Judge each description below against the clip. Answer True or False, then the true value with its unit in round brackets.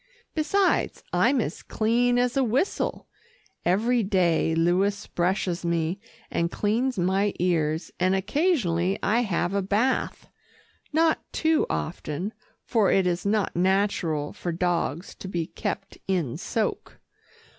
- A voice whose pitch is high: True (195 Hz)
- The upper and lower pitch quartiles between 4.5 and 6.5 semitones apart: True (5.0 semitones)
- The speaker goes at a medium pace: False (125 wpm)